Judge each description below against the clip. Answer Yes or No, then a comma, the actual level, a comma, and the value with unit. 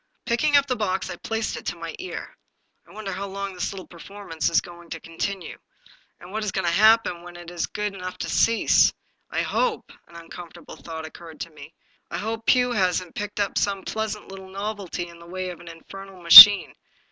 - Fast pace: Yes, fast, 230 wpm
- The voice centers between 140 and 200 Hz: Yes, high, 190 Hz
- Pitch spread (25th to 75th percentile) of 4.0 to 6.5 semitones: No, average, 3.4 semitones